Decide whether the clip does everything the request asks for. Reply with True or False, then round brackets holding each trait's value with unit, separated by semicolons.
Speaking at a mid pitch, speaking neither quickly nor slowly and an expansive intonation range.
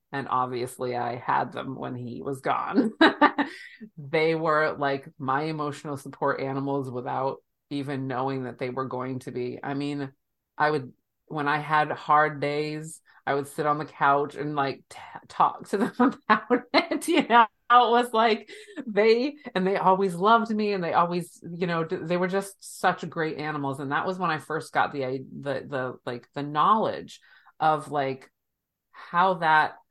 True (150 Hz; 175 wpm; 6.2 semitones)